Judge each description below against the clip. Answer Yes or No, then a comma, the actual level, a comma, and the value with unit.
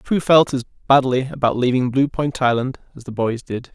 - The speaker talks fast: Yes, fast, 210 wpm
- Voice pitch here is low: Yes, low, 130 Hz